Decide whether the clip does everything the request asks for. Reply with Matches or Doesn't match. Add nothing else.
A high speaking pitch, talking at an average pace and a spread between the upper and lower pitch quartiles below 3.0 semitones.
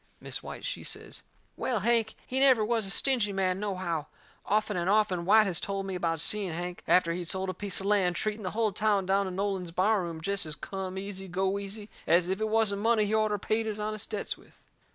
Doesn't match